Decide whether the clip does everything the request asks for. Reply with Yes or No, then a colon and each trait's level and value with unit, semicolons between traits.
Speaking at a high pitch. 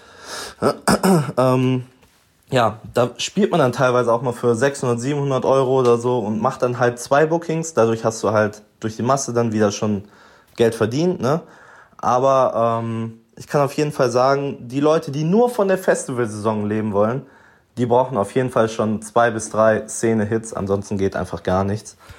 No: low, 120 Hz